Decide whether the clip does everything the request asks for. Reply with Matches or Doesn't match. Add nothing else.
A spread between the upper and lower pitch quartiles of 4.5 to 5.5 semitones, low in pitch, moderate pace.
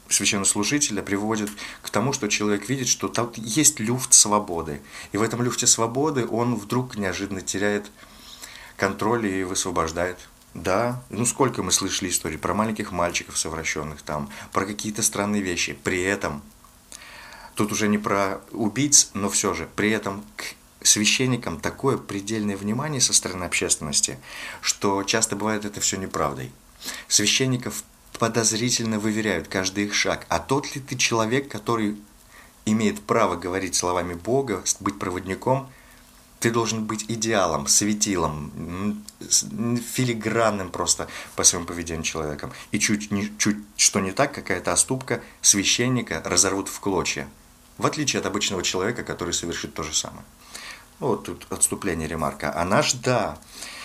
Doesn't match